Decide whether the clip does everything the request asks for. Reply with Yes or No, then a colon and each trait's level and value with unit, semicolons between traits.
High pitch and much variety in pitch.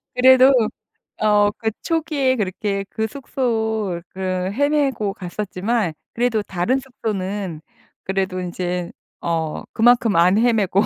No: high, 210 Hz; average, 4.7 semitones